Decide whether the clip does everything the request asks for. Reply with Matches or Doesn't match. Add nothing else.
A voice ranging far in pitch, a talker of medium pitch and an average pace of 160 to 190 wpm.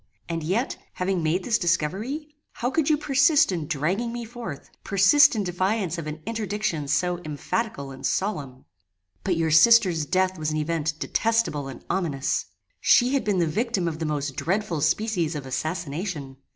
Matches